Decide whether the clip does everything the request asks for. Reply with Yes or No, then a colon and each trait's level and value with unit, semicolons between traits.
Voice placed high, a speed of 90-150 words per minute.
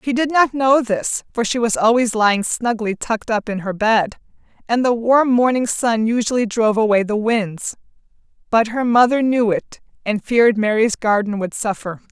No: high, 225 Hz; average, 185 wpm